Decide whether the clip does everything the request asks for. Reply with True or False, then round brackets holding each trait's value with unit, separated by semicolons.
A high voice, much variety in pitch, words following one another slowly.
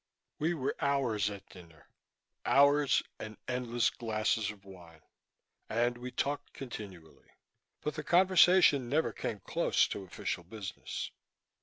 False (120 Hz; 6.2 semitones; 125 wpm)